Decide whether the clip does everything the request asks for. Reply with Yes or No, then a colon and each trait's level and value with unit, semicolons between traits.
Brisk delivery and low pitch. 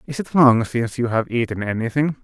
Yes: fast, 215 wpm; low, 120 Hz